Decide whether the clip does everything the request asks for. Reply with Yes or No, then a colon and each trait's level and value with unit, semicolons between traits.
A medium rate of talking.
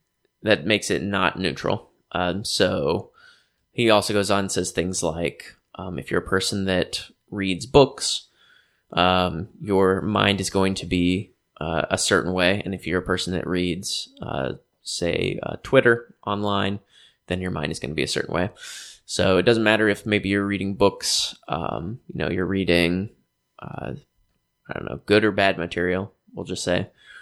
Yes: average, 180 wpm